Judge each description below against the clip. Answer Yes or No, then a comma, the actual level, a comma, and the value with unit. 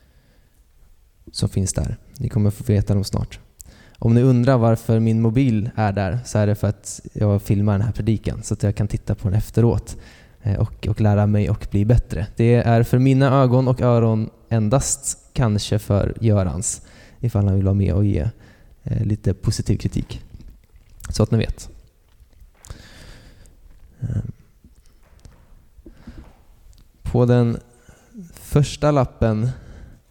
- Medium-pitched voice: No, low, 110 Hz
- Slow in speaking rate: No, average, 145 wpm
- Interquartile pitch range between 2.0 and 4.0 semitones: Yes, average, 2.8 semitones